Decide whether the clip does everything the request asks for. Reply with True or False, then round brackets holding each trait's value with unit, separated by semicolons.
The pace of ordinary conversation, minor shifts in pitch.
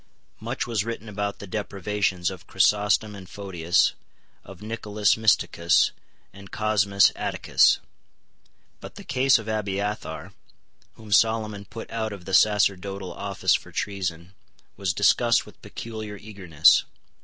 False (125 wpm; 2.2 semitones)